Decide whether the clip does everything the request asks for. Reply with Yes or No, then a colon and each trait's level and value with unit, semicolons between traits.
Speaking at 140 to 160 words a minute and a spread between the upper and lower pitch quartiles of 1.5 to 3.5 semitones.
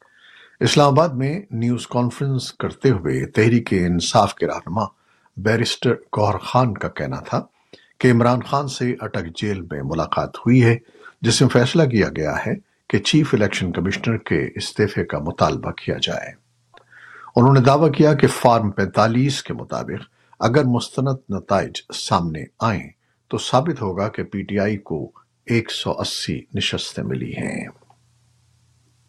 No: average, 145 wpm; average, 4.5 semitones